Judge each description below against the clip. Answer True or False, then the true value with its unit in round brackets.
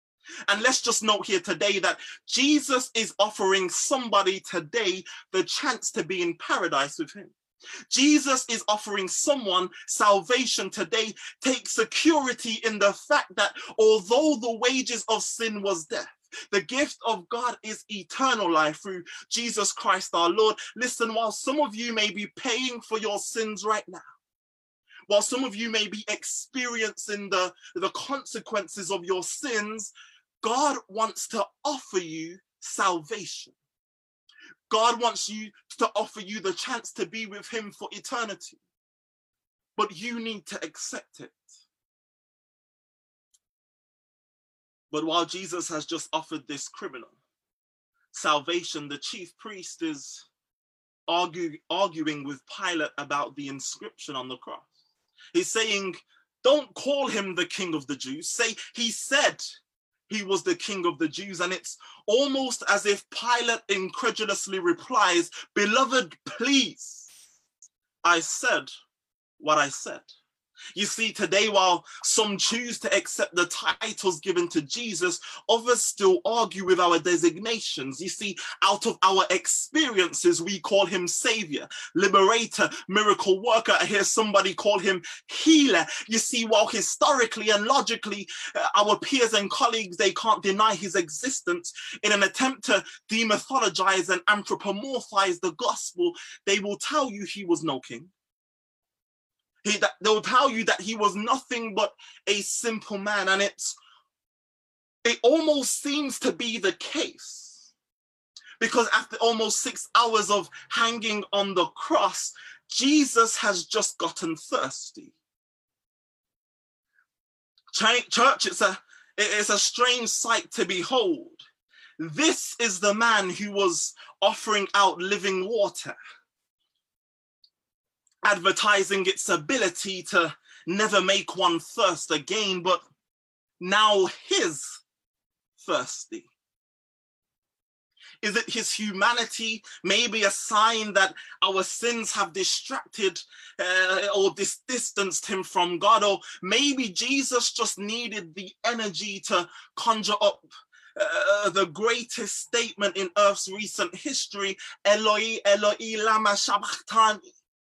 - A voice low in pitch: False (215 Hz)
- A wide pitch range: False (4.4 semitones)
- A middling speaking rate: False (130 wpm)